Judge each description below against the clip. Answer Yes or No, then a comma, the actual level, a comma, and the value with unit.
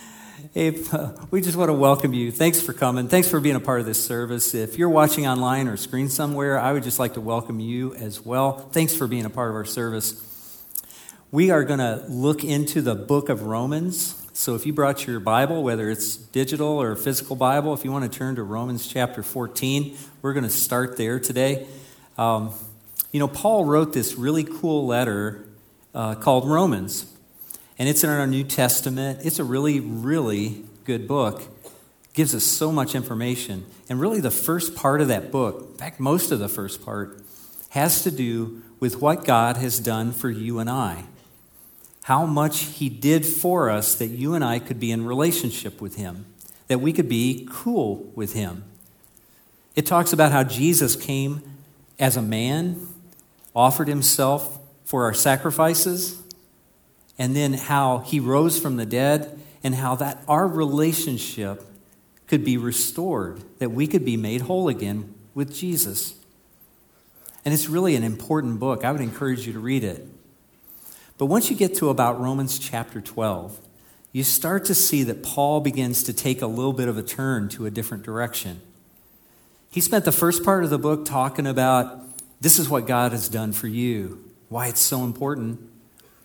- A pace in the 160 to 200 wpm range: Yes, average, 180 wpm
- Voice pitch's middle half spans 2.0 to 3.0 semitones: No, average, 4.4 semitones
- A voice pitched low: Yes, low, 130 Hz